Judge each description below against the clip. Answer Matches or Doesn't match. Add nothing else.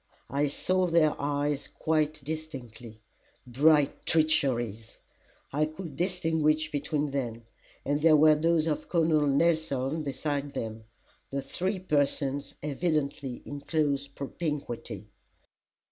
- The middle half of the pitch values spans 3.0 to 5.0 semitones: Doesn't match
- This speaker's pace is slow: Matches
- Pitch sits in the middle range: Matches